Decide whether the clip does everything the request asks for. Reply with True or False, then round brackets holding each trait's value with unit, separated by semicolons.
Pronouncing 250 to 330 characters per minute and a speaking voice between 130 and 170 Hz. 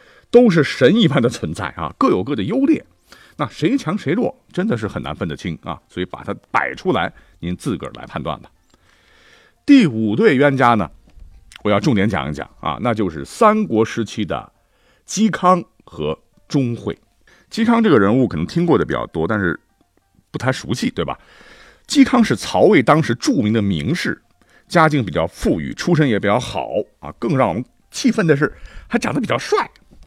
True (265 characters per minute; 135 Hz)